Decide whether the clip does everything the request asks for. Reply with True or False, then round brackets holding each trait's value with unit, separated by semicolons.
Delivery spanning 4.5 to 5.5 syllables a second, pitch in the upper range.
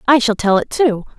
True (5.3 syllables/s; 235 Hz)